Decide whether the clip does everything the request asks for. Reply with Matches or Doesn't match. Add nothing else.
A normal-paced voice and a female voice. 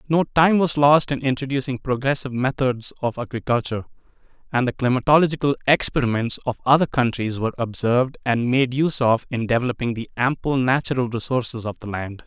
Doesn't match